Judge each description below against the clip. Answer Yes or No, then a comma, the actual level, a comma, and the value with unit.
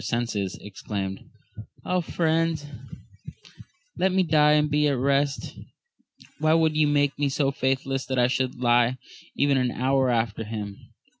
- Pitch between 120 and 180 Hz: Yes, low, 135 Hz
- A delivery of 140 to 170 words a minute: Yes, average, 150 wpm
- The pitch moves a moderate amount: Yes, average, 3.7 semitones